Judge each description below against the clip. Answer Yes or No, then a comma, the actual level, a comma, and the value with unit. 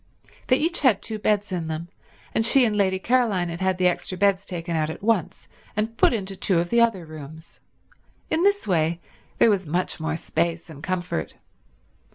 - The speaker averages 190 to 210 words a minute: Yes, average, 195 wpm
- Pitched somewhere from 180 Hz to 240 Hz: Yes, medium, 185 Hz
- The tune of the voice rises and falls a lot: No, average, 4.5 semitones